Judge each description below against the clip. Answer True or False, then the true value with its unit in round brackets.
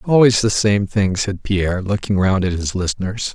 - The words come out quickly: False (195 wpm)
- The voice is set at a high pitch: False (100 Hz)